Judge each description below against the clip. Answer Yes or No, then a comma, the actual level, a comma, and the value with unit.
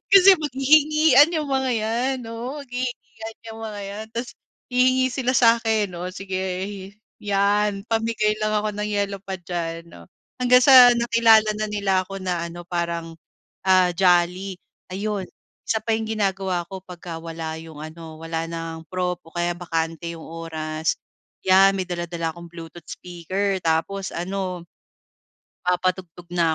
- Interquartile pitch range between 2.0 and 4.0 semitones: No, average, 4.6 semitones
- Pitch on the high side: Yes, high, 195 Hz